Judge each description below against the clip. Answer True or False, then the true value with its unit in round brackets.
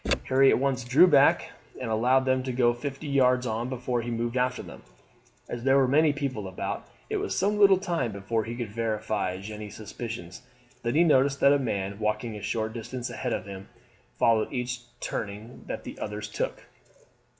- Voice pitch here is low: True (120 Hz)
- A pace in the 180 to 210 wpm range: True (190 wpm)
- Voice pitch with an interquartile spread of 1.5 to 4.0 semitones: True (3.5 semitones)